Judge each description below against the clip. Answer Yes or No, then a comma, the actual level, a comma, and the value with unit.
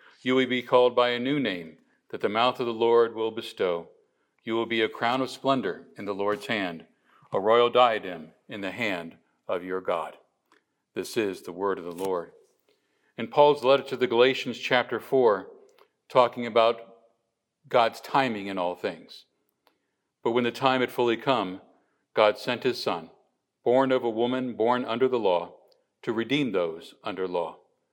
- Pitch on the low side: Yes, low, 120 Hz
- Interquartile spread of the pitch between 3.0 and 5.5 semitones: No, narrow, 2.4 semitones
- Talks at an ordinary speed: Yes, average, 175 wpm